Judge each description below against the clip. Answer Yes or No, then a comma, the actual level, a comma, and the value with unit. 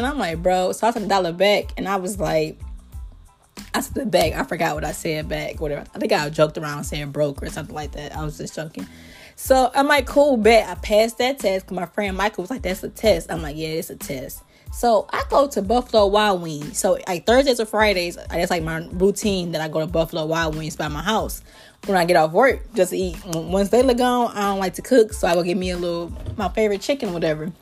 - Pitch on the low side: No, high, 190 Hz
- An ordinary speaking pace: No, fast, 255 wpm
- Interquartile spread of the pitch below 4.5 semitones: No, average, 5.1 semitones